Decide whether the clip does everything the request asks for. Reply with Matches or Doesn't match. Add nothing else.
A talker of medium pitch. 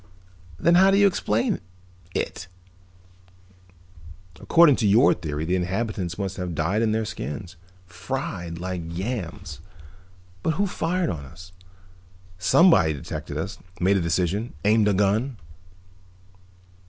Doesn't match